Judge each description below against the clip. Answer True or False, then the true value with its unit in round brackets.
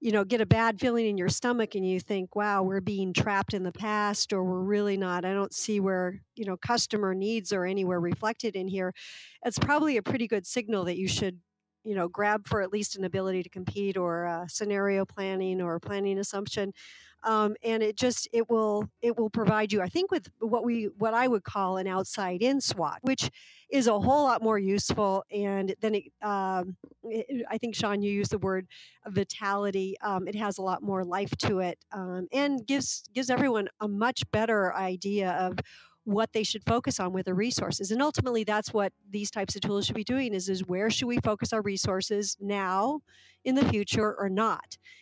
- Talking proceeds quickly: True (210 wpm)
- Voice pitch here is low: False (205 Hz)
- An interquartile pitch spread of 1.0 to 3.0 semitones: True (2.7 semitones)